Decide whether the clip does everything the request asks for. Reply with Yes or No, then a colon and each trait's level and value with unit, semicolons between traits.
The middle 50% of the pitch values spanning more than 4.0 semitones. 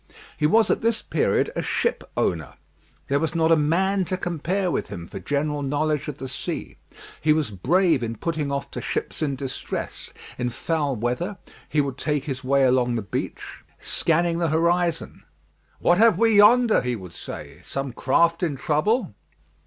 Yes: average, 4.5 semitones